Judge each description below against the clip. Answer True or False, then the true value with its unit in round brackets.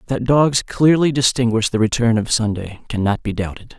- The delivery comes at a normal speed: True (175 wpm)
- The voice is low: True (115 Hz)